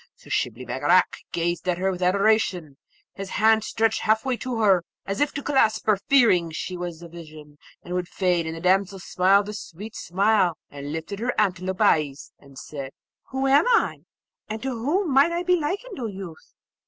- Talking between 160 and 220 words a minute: Yes, average, 190 wpm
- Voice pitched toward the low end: No, high, 195 Hz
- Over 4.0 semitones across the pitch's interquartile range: Yes, average, 4.6 semitones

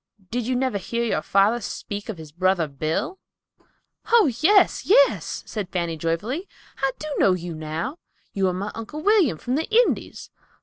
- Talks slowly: No, average, 170 wpm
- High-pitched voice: Yes, high, 220 Hz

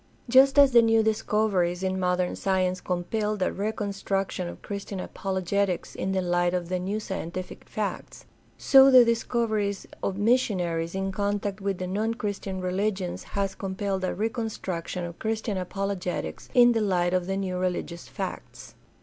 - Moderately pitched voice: No, high, 195 Hz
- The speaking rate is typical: Yes, average, 160 wpm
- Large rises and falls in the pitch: No, average, 2.8 semitones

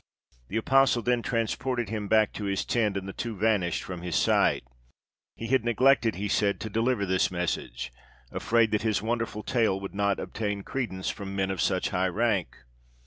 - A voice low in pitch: Yes, low, 105 Hz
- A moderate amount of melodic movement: Yes, average, 3.1 semitones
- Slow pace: No, average, 185 wpm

